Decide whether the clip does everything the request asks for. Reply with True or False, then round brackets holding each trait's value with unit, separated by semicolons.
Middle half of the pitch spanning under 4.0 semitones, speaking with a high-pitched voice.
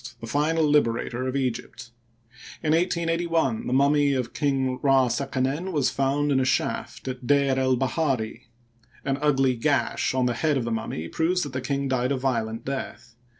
False (2.5 semitones; 135 Hz)